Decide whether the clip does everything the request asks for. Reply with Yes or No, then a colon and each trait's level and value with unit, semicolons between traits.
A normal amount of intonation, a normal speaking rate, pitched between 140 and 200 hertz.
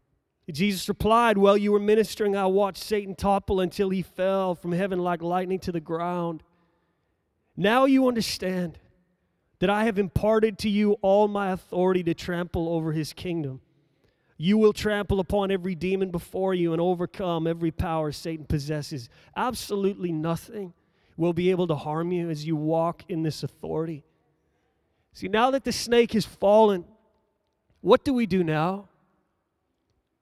Yes: average, 3.6 semitones; average, 155 wpm; medium, 185 Hz